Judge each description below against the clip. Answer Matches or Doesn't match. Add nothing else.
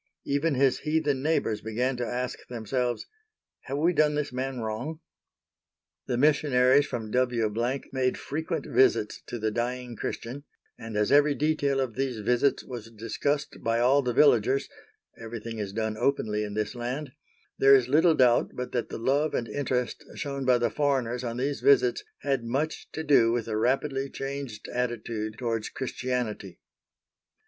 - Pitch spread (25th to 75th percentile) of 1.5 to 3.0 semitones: Doesn't match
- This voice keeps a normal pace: Matches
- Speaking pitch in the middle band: Doesn't match